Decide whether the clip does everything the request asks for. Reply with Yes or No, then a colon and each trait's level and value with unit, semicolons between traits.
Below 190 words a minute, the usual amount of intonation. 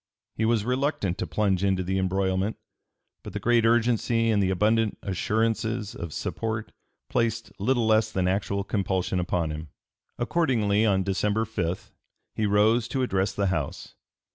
Yes: average, 150 wpm; average, 3.0 semitones